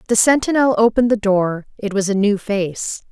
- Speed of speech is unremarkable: Yes, average, 190 wpm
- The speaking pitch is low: No, high, 215 Hz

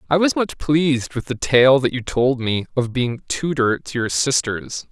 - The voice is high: No, low, 130 Hz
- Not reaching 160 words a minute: No, fast, 205 wpm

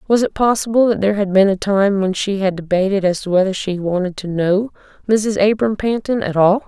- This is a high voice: Yes, high, 200 Hz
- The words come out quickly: Yes, fast, 225 wpm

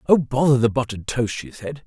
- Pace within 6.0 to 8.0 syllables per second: No, 5.8 syllables/s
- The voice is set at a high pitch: No, low, 125 Hz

